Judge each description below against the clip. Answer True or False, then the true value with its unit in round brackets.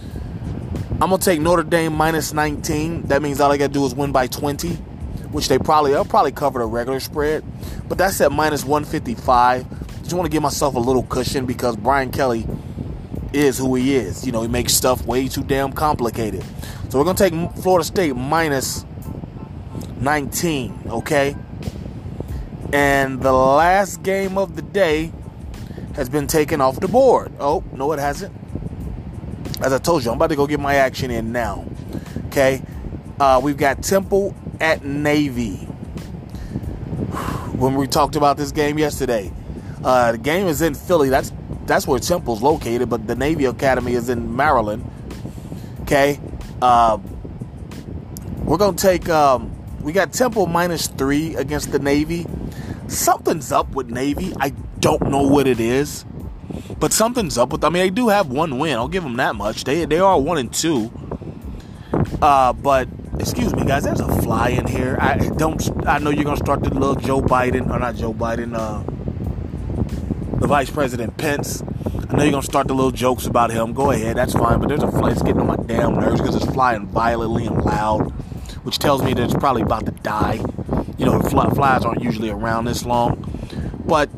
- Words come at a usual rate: True (180 wpm)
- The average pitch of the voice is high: False (140 Hz)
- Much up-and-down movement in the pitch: False (3.8 semitones)